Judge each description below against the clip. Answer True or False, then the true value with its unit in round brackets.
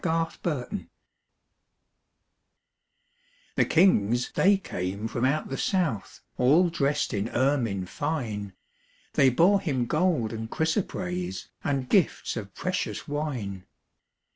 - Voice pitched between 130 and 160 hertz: True (140 Hz)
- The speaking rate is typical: False (110 wpm)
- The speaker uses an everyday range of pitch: False (6.8 semitones)